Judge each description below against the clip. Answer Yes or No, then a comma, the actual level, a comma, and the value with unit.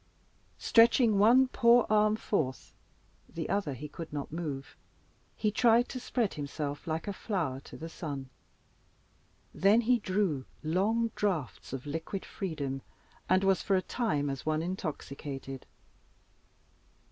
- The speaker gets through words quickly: No, slow, 135 wpm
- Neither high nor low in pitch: Yes, medium, 175 Hz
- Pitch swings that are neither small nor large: No, wide, 6.6 semitones